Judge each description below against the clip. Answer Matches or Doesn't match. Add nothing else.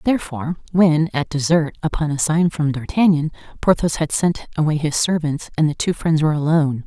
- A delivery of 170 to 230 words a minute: Matches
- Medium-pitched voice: Matches